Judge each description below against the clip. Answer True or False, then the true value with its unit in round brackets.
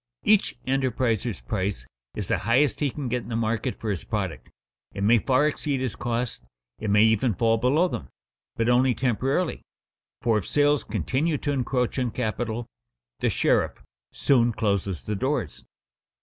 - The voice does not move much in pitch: False (3.4 semitones)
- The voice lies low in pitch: True (120 Hz)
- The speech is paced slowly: False (165 wpm)